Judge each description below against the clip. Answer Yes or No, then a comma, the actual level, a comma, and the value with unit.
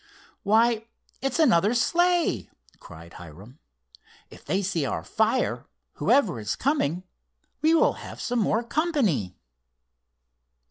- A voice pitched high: Yes, high, 220 Hz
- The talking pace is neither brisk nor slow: No, slow, 110 wpm